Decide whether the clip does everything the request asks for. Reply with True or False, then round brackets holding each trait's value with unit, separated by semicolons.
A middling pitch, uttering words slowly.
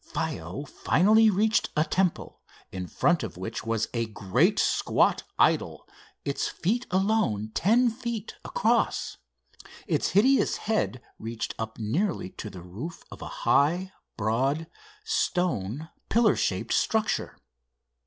True (165 Hz; 125 wpm)